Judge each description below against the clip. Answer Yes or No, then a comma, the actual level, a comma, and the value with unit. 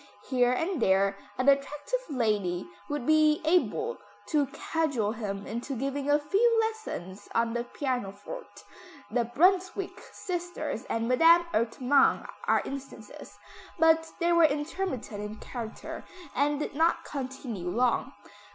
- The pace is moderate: No, slow, 125 wpm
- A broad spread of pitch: Yes, wide, 5.8 semitones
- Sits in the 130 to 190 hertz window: No, very high, 275 Hz